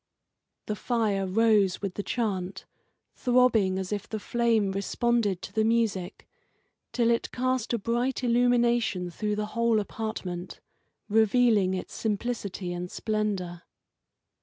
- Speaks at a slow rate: Yes, slow, 125 wpm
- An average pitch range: Yes, average, 3.6 semitones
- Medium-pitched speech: No, high, 215 Hz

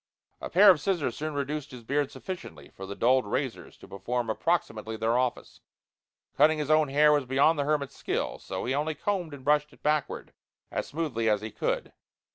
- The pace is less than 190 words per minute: No, average, 195 wpm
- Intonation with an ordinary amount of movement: Yes, average, 4.2 semitones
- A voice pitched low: No, medium, 145 Hz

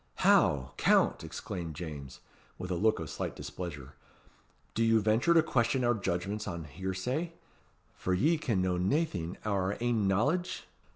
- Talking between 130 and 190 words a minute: Yes, average, 155 wpm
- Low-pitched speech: Yes, low, 100 Hz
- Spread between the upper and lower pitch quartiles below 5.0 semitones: No, wide, 5.4 semitones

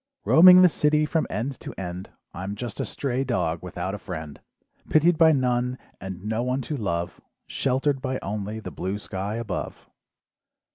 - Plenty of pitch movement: Yes, wide, 6.3 semitones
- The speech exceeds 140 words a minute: Yes, average, 165 wpm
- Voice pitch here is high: No, low, 115 Hz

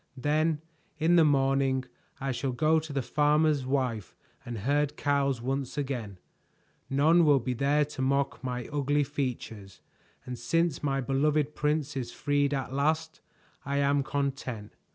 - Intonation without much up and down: Yes, narrow, 2.2 semitones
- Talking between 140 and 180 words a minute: Yes, average, 150 wpm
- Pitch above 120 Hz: Yes, medium, 140 Hz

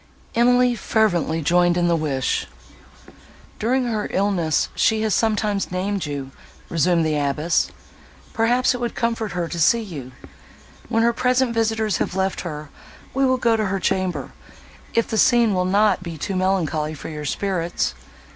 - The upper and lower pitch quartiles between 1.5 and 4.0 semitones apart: No, average, 5.2 semitones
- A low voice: No, high, 195 Hz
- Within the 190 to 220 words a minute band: No, average, 160 wpm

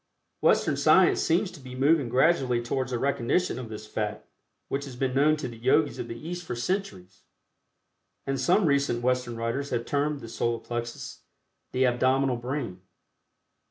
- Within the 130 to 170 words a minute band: Yes, average, 165 wpm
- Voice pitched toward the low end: Yes, low, 130 Hz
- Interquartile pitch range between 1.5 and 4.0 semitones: Yes, average, 3.2 semitones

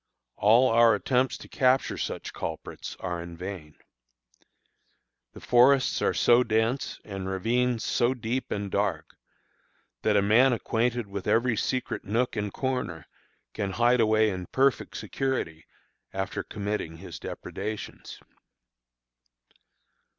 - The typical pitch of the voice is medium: No, low, 110 Hz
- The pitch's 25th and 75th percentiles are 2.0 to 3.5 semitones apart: No, average, 4.2 semitones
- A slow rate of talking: Yes, slow, 120 wpm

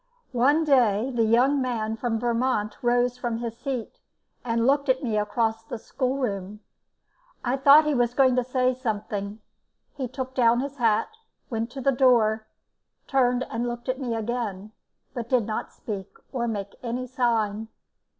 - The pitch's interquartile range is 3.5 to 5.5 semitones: No, narrow, 2.6 semitones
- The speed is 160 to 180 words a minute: Yes, average, 165 wpm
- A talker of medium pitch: No, high, 240 Hz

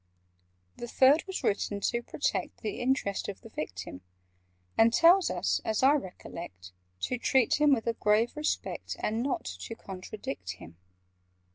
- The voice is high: Yes, high, 225 Hz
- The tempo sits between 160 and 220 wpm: No, average, 150 wpm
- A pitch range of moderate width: No, wide, 6.4 semitones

